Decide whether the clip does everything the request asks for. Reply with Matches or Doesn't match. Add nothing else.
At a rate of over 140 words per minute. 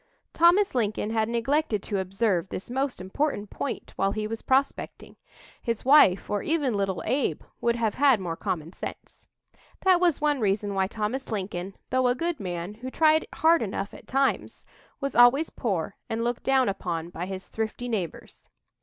Matches